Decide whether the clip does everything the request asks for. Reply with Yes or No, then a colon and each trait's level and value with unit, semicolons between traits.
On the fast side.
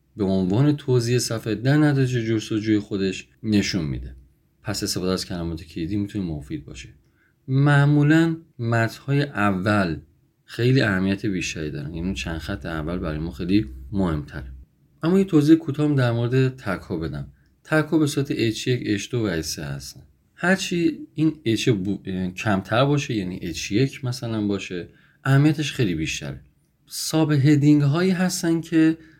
No: average, 140 wpm